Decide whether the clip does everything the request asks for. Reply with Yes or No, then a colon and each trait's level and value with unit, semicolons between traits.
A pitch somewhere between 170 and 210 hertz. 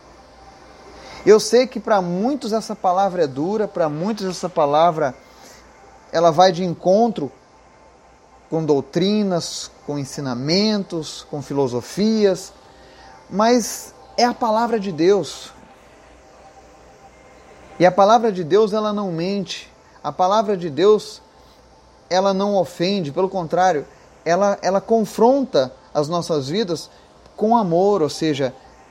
Yes: medium, 185 Hz